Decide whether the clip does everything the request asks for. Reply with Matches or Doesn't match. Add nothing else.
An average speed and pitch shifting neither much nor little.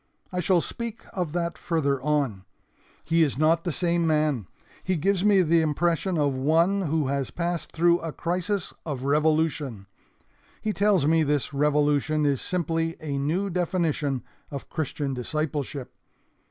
Matches